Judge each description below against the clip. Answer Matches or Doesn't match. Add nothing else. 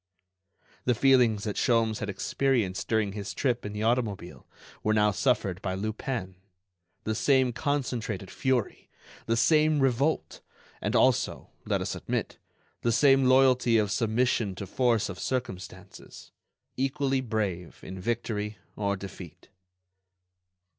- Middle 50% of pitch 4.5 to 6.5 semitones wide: Doesn't match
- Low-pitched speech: Matches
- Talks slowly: Matches